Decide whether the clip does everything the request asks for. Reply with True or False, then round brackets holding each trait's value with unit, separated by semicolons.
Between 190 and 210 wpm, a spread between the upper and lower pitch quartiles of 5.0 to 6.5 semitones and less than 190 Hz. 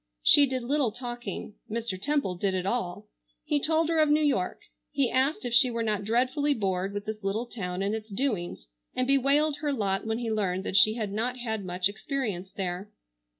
False (200 wpm; 5.3 semitones; 225 Hz)